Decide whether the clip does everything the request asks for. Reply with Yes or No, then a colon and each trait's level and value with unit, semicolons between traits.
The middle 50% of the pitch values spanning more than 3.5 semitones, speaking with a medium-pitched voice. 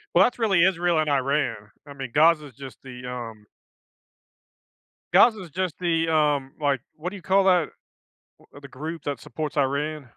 Yes: average, 4.0 semitones; medium, 150 Hz